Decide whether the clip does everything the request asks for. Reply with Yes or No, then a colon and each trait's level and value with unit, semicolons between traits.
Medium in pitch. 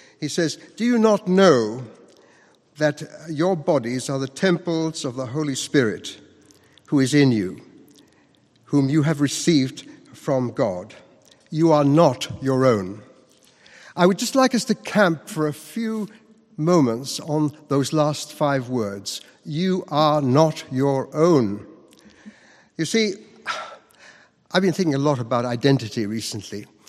Yes: medium, 150 Hz